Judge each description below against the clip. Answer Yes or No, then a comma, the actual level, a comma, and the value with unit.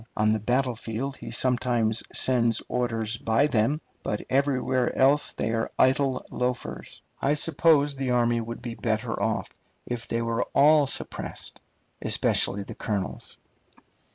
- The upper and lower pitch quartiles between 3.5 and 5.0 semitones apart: No, average, 3.1 semitones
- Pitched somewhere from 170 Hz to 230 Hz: No, low, 120 Hz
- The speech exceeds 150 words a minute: No, slow, 135 wpm